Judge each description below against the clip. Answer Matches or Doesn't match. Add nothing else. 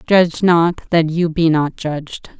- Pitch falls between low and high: Matches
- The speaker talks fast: Doesn't match